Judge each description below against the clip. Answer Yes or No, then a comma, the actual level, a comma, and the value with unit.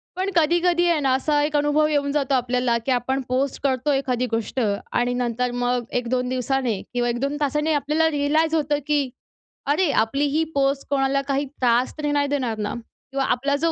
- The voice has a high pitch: Yes, very high, 275 Hz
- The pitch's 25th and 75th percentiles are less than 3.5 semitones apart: Yes, average, 2.8 semitones